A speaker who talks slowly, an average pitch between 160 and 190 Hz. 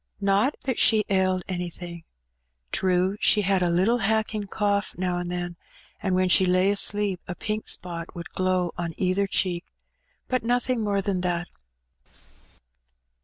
No: average, 150 wpm; medium, 185 Hz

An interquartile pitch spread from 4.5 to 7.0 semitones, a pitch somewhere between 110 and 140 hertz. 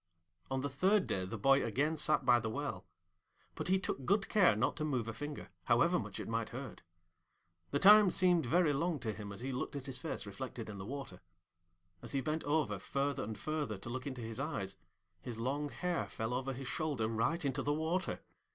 Yes: average, 5.2 semitones; low, 135 Hz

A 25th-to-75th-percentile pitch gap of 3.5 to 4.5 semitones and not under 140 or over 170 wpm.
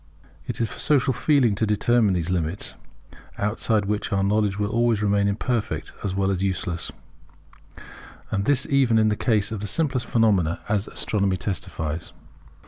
No: average, 2.9 semitones; average, 160 wpm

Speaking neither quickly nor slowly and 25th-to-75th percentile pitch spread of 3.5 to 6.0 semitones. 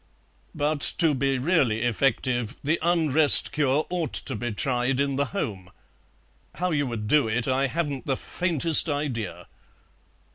Yes: average, 145 wpm; average, 4.0 semitones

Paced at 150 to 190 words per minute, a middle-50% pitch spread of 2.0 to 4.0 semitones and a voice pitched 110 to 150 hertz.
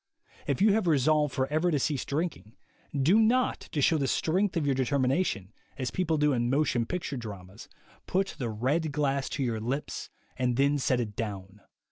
No: average, 185 wpm; average, 4.6 semitones; medium, 140 Hz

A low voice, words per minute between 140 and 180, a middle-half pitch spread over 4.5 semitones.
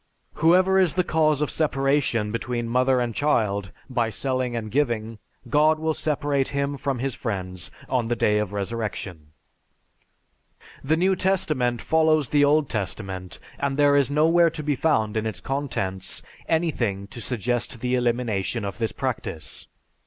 Yes: low, 125 Hz; average, 155 wpm; average, 5.2 semitones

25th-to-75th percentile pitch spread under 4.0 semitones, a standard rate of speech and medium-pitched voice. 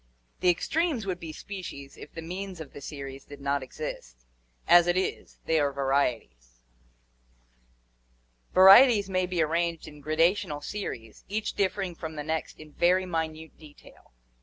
No: average, 4.6 semitones; average, 160 wpm; medium, 160 Hz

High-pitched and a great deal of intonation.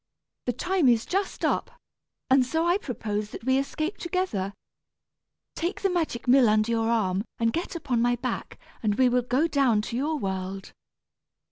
Yes: very high, 250 Hz; wide, 6.2 semitones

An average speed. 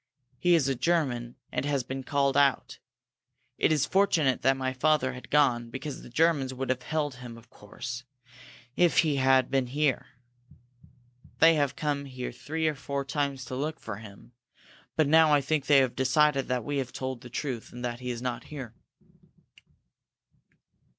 Yes: average, 175 wpm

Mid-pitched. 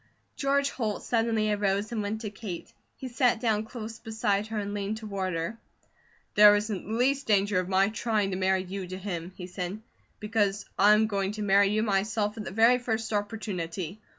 No: high, 210 Hz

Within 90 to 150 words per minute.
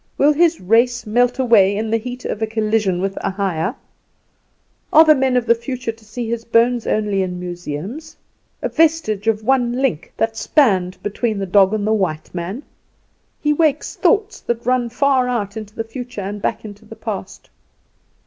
No: average, 185 wpm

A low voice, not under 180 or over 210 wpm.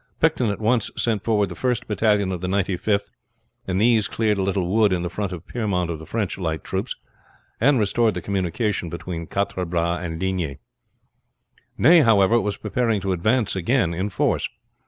Yes: low, 100 Hz; average, 185 wpm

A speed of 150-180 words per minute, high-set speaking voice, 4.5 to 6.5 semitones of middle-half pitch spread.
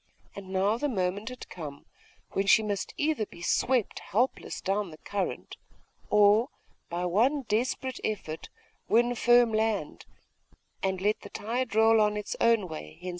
No: average, 155 wpm; high, 210 Hz; average, 3.7 semitones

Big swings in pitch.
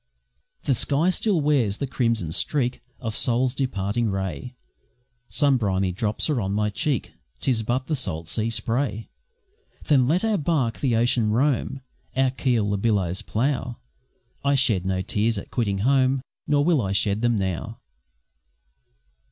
No: average, 4.8 semitones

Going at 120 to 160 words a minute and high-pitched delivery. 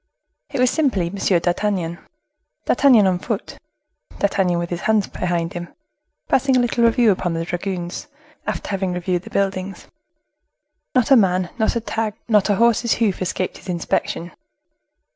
Yes: average, 155 wpm; high, 195 Hz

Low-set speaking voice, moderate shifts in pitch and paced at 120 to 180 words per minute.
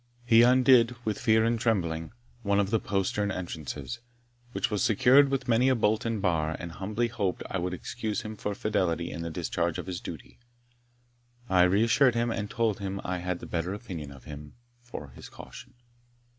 No: low, 100 Hz; average, 4.8 semitones; average, 190 wpm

